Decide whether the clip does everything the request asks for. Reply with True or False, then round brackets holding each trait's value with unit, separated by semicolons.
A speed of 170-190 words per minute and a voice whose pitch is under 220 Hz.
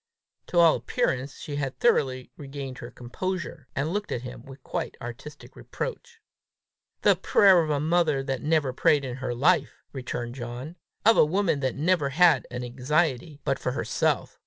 True (180 wpm; 140 Hz)